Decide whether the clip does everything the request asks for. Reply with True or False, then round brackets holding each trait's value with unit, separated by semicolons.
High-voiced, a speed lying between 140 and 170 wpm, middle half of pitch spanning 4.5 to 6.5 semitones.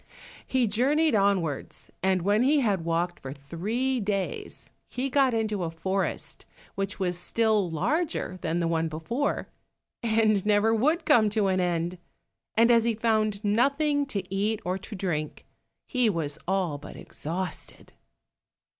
True (205 Hz; 145 wpm; 4.8 semitones)